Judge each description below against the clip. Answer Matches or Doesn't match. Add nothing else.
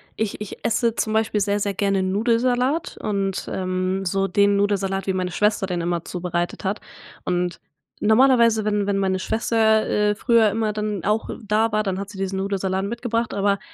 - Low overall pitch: Doesn't match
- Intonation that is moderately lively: Doesn't match